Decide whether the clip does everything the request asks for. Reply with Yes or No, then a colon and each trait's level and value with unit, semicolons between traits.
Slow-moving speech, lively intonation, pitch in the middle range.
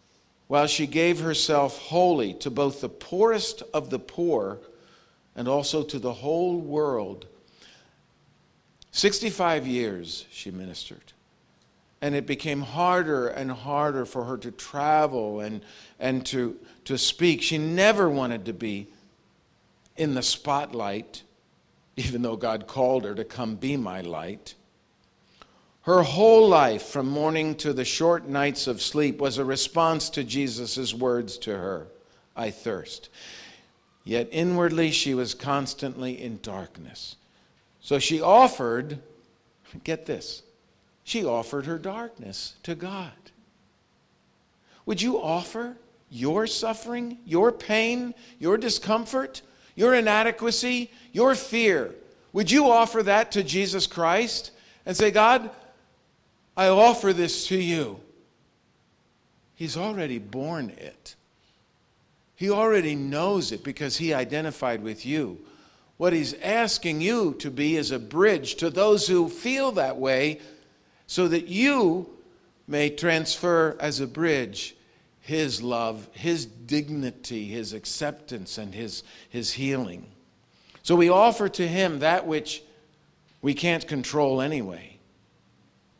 Yes: slow, 125 wpm; wide, 6.3 semitones; medium, 150 Hz